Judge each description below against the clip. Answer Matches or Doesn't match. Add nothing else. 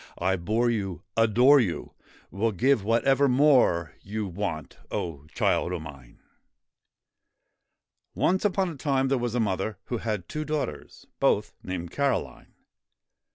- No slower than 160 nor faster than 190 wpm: Doesn't match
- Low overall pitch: Matches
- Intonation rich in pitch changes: Matches